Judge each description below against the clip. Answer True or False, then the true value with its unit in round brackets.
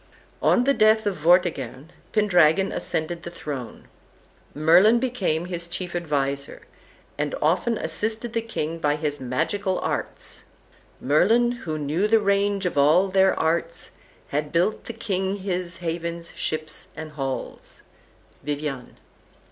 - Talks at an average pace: False (130 wpm)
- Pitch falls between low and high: True (170 Hz)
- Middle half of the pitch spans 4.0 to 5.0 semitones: True (4.7 semitones)